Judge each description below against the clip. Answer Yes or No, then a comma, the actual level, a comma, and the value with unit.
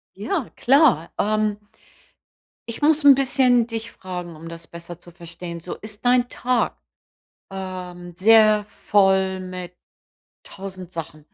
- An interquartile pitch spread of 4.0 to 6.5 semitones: Yes, average, 4.6 semitones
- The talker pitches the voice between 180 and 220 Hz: Yes, high, 190 Hz